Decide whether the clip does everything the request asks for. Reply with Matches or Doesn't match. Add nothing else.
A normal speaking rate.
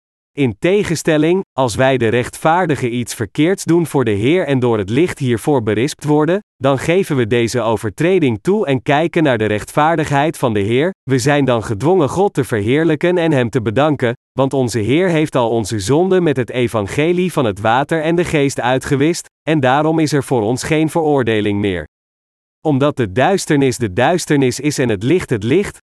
Matches